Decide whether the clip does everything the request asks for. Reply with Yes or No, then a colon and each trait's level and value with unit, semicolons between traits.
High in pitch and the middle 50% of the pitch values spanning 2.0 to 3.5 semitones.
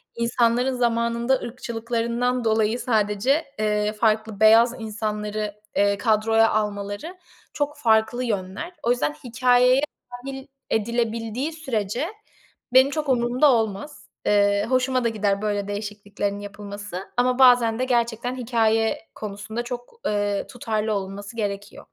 Yes: high, 225 Hz; average, 3.0 semitones